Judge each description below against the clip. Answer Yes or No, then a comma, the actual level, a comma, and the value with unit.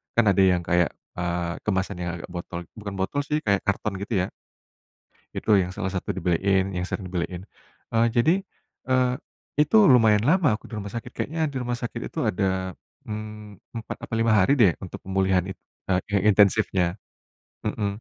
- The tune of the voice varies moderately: Yes, average, 3.6 semitones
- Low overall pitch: Yes, low, 100 Hz